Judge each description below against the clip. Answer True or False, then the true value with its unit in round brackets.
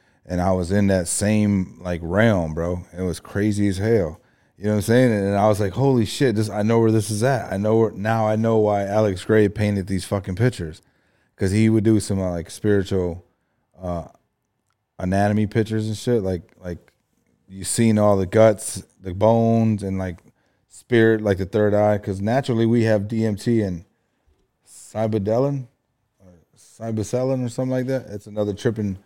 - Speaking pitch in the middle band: False (105 Hz)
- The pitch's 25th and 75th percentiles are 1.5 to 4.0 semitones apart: True (2.8 semitones)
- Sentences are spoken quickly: False (185 wpm)